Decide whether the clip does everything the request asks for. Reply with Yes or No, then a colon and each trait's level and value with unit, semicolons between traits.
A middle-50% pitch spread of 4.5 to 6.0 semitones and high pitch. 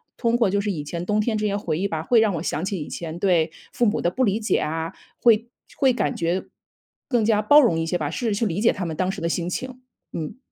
Yes: average, 5.1 semitones; high, 200 Hz